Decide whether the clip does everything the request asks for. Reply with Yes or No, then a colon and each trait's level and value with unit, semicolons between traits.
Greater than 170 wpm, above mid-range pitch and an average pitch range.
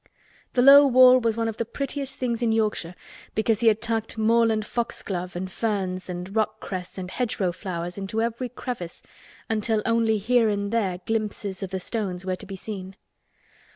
Yes: average, 180 wpm; high, 215 Hz; average, 3.4 semitones